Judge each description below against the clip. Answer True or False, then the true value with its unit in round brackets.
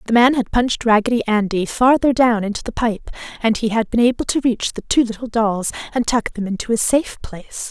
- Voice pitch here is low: False (230 Hz)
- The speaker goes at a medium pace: False (225 wpm)